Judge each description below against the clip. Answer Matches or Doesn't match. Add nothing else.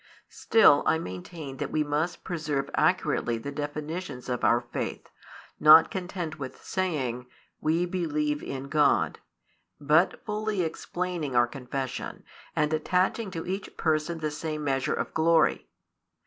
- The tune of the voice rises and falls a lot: Doesn't match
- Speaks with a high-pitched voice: Doesn't match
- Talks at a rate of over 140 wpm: Doesn't match